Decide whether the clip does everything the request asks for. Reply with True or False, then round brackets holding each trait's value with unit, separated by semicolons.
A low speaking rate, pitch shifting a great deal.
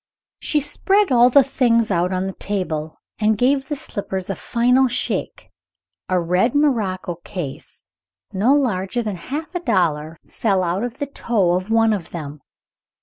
False (160 wpm; 5.8 semitones)